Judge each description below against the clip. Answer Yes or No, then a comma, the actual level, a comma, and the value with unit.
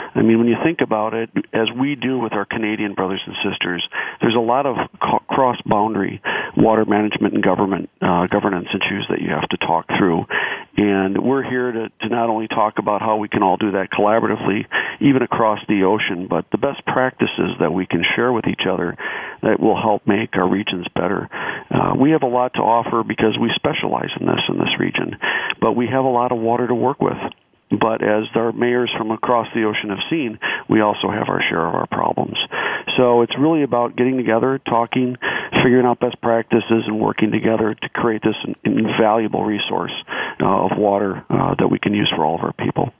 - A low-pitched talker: Yes, low, 115 Hz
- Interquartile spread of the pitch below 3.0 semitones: Yes, narrow, 2.6 semitones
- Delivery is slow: No, fast, 205 wpm